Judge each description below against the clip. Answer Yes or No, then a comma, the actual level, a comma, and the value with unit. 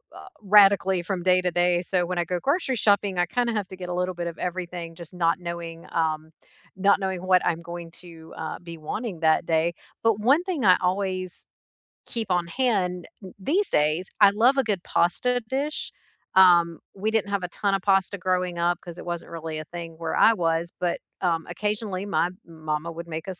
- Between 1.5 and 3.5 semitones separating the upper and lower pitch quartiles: Yes, average, 2.9 semitones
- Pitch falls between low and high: Yes, medium, 180 Hz